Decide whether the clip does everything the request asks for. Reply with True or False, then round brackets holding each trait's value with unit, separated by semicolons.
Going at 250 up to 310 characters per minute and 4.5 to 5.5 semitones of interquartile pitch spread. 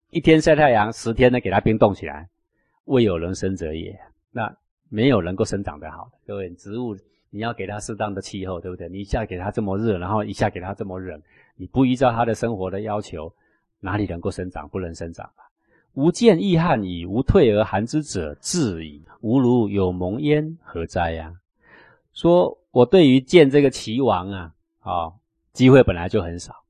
True (280 characters per minute; 5.2 semitones)